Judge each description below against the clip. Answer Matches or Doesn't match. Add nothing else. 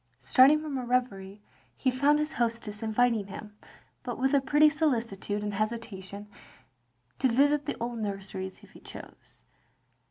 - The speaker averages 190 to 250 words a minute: Doesn't match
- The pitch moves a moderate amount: Matches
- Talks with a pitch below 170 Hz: Doesn't match